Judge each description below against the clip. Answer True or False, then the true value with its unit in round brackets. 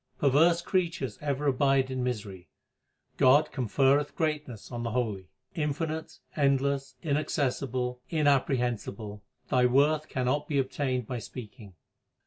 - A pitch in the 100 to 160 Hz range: True (135 Hz)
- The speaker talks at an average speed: False (115 wpm)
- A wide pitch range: False (3.0 semitones)